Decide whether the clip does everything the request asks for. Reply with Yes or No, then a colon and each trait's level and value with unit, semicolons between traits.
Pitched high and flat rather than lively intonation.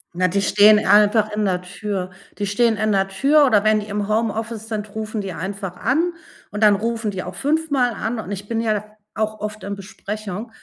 Yes: high, 210 Hz; narrow, 1.9 semitones